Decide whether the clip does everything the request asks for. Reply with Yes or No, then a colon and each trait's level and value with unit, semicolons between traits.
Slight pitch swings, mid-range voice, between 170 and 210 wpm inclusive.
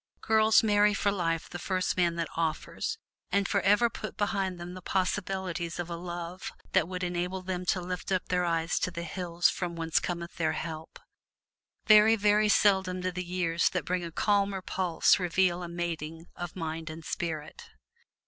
Yes: narrow, 2.2 semitones; medium, 180 Hz; average, 175 wpm